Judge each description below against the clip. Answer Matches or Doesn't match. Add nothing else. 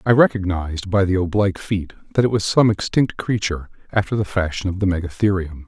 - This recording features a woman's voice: Doesn't match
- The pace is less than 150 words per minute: Doesn't match